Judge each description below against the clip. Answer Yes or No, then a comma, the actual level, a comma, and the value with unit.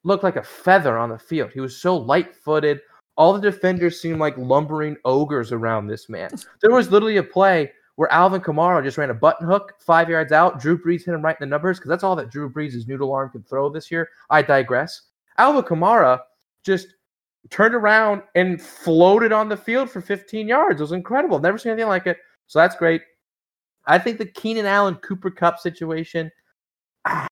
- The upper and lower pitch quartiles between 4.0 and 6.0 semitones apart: Yes, average, 4.7 semitones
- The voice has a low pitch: No, medium, 170 Hz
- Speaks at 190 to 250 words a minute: Yes, average, 200 wpm